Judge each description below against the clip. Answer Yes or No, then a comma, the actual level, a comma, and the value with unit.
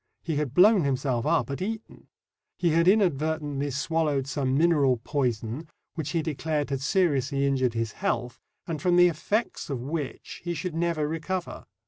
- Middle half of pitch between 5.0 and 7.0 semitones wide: No, average, 3.8 semitones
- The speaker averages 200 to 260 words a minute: No, average, 160 wpm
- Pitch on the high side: No, medium, 150 Hz